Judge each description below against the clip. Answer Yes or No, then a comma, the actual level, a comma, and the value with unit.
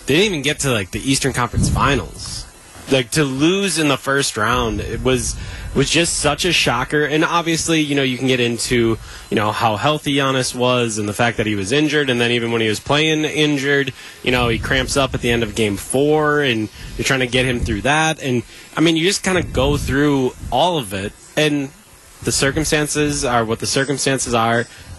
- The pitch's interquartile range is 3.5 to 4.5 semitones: Yes, average, 4.2 semitones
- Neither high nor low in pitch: No, low, 130 Hz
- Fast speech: Yes, fast, 225 wpm